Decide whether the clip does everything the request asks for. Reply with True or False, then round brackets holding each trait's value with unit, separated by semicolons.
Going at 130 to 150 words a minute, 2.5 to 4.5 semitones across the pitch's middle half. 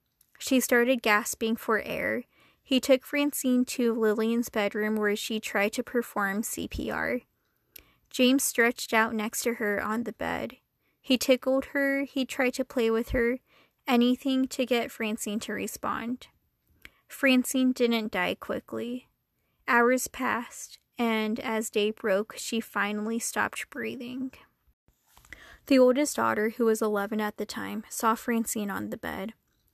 True (140 wpm; 2.9 semitones)